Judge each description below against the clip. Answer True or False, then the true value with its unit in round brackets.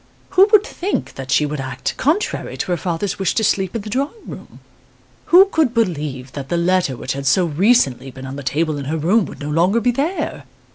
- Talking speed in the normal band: False (225 wpm)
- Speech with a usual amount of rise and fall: False (8.8 semitones)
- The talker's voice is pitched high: False (175 Hz)